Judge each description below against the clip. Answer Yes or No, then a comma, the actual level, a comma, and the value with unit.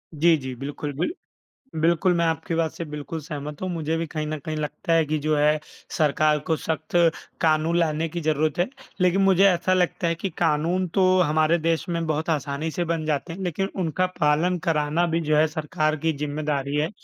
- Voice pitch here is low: No, medium, 160 Hz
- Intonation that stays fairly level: Yes, narrow, 2.1 semitones